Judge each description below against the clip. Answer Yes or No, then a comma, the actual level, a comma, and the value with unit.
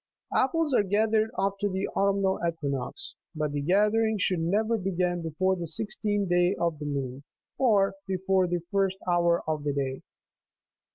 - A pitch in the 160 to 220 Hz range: Yes, high, 190 Hz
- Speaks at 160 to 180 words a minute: Yes, average, 165 wpm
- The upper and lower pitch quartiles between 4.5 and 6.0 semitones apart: No, average, 3.7 semitones